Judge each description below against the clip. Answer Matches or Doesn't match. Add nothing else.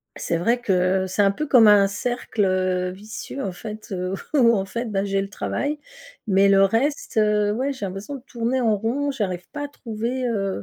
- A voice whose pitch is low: Doesn't match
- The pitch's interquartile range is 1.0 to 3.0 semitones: Doesn't match